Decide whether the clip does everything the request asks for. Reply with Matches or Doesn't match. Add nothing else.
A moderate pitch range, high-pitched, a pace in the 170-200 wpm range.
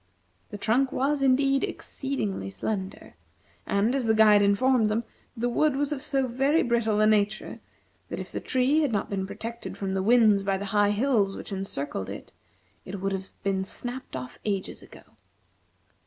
Matches